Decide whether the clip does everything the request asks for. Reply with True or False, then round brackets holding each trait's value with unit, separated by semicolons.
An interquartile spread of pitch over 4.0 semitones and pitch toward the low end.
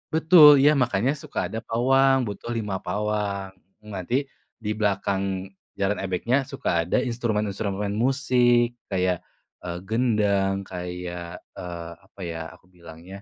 True (4.5 semitones; 105 Hz)